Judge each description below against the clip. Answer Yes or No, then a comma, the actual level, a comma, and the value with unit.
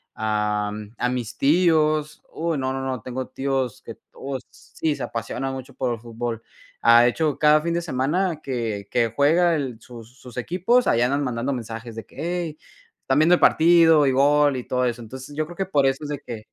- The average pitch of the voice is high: No, low, 135 Hz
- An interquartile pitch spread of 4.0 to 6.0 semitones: Yes, average, 4.3 semitones